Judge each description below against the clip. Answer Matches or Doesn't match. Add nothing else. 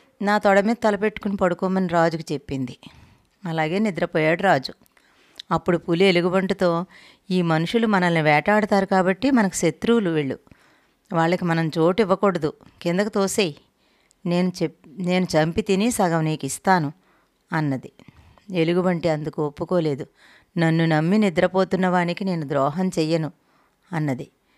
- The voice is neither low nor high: Matches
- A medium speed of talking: Matches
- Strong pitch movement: Doesn't match